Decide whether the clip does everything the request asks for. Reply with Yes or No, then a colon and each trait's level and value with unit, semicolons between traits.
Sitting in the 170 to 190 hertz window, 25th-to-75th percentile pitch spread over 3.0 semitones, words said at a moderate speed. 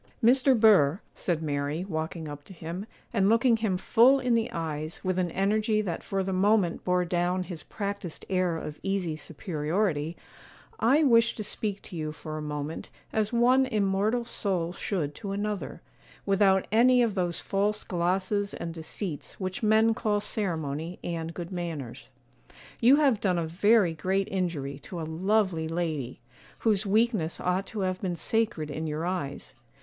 Yes: medium, 185 Hz; average, 4.6 semitones; average, 165 wpm